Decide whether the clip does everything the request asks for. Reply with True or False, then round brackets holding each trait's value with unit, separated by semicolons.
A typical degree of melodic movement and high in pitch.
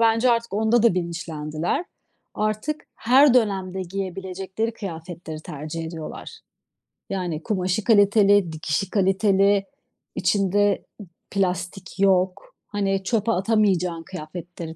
True (3.0 semitones; 195 Hz)